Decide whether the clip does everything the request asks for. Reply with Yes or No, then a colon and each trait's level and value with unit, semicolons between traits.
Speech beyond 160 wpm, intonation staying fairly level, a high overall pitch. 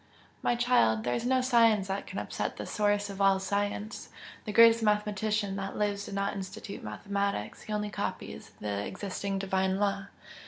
Yes: average, 170 wpm; narrow, 1.6 semitones; high, 200 Hz